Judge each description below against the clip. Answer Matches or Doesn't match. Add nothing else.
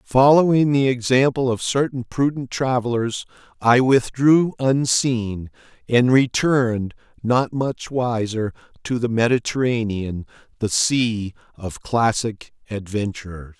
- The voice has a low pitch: Matches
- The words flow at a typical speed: Doesn't match